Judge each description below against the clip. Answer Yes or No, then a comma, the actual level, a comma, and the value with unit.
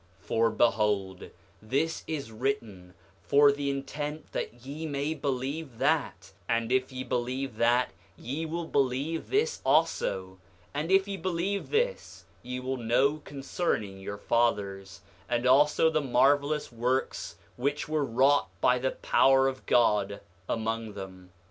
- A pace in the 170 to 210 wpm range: No, average, 140 wpm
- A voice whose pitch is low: Yes, low, 130 Hz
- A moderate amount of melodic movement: Yes, average, 4.5 semitones